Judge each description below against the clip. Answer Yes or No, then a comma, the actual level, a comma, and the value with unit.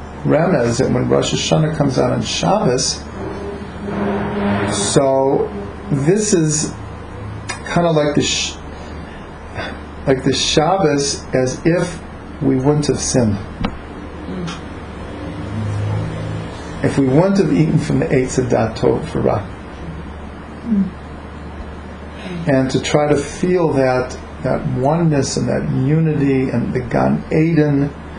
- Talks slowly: Yes, slow, 115 wpm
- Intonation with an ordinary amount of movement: No, wide, 8.9 semitones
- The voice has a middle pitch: No, low, 110 Hz